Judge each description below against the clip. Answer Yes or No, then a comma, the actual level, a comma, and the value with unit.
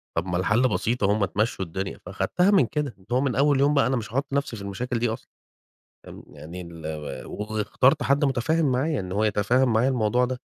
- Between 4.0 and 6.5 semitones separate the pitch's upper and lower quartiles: Yes, average, 4.8 semitones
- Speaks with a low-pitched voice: Yes, low, 120 Hz